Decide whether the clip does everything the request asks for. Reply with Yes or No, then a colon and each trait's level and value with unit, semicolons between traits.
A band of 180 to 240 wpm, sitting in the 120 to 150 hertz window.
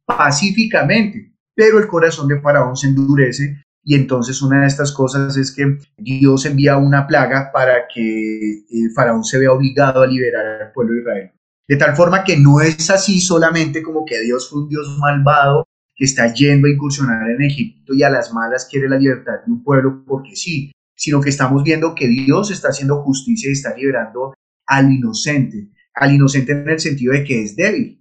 Yes: fast, 190 wpm; medium, 140 Hz